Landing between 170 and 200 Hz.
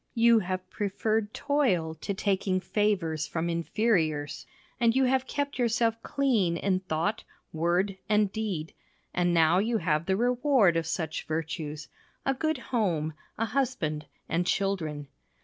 Yes: high, 190 Hz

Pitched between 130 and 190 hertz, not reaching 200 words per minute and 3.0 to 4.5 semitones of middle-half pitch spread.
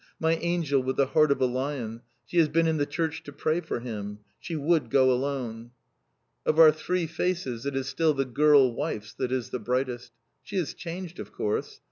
No: medium, 140 Hz; fast, 205 wpm; average, 4.2 semitones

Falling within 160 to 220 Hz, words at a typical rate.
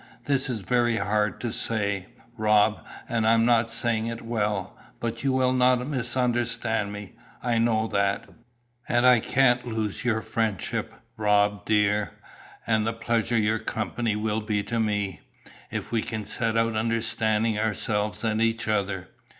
No: low, 110 Hz; average, 155 wpm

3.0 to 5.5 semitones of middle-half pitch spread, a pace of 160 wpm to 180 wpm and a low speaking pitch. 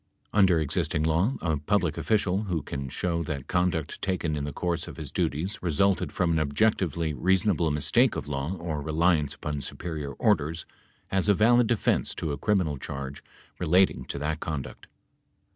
Yes: average, 3.9 semitones; average, 170 wpm; very low, 80 Hz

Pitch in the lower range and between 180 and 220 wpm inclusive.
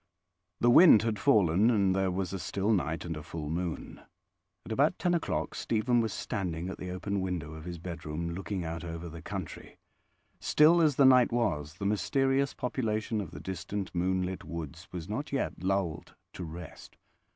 Yes: very low, 95 Hz; average, 185 wpm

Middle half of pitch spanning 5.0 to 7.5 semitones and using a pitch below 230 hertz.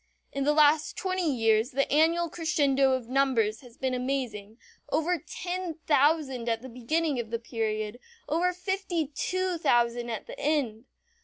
No: wide, 5.4 semitones; very high, 275 Hz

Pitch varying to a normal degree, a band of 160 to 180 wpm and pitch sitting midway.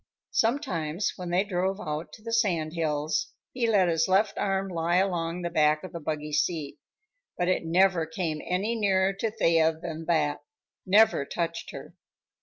Yes: average, 3.3 semitones; average, 170 wpm; medium, 175 Hz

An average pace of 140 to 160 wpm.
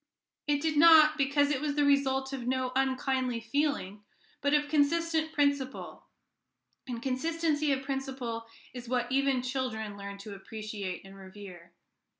Yes: average, 145 wpm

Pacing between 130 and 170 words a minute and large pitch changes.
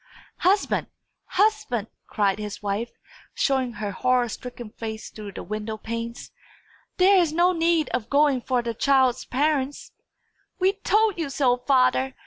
Yes: average, 140 wpm; wide, 5.8 semitones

